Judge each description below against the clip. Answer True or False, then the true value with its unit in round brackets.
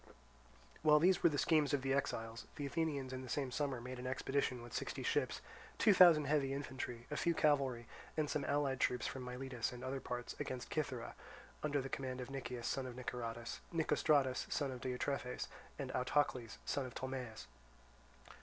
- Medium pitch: False (130 Hz)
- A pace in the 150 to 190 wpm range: True (180 wpm)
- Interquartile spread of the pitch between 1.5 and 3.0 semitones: True (2.5 semitones)